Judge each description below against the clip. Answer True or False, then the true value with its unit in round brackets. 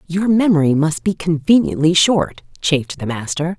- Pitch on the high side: False (160 Hz)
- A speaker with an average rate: True (150 wpm)